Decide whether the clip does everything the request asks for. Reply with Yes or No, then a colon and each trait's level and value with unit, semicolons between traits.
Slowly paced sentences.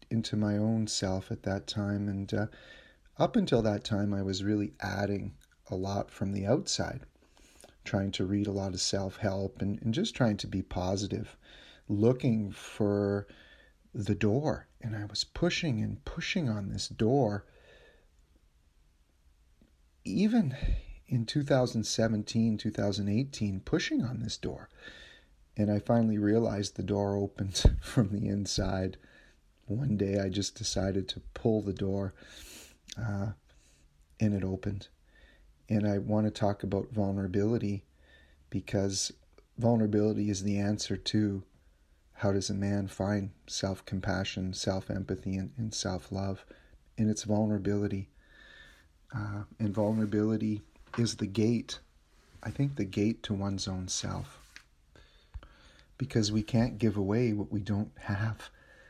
Yes: slow, 130 wpm